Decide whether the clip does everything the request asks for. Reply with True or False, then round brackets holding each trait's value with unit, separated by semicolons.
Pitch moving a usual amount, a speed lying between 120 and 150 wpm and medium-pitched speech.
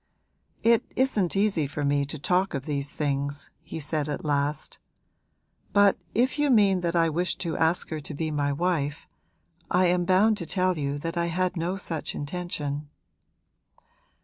False (4.1 semitones; 170 wpm; 165 Hz)